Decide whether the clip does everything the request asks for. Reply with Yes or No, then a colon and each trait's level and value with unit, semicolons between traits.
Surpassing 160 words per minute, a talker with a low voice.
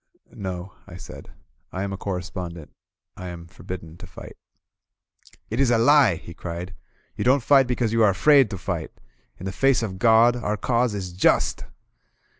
Yes: average, 180 wpm; low, 100 Hz